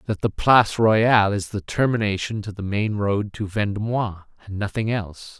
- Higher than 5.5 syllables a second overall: No, 5.1 syllables/s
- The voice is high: No, low, 105 Hz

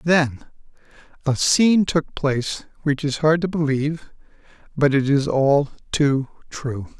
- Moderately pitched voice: Yes, medium, 145 Hz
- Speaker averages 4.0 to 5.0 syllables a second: Yes, 4.3 syllables/s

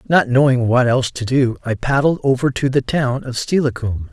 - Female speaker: No, male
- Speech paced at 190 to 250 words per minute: Yes, fast, 205 wpm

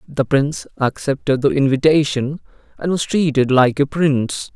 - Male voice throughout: Yes, male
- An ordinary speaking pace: Yes, average, 145 wpm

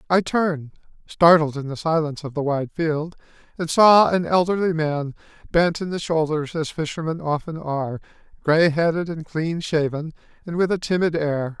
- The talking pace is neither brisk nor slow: Yes, average, 170 wpm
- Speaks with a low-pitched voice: No, medium, 160 Hz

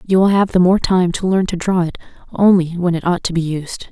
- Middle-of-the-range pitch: Yes, medium, 180 Hz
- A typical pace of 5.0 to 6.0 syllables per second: Yes, 5.5 syllables/s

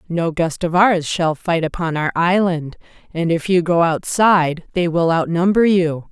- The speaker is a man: No, female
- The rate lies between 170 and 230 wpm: Yes, average, 175 wpm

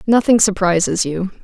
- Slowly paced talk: Yes, slow, 125 wpm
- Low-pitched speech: No, high, 195 Hz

